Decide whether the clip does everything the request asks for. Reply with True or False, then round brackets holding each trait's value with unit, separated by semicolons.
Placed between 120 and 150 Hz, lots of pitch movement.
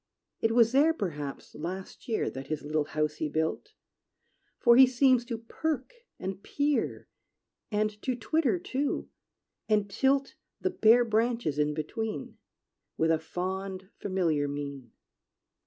False (205 Hz; 7.7 semitones)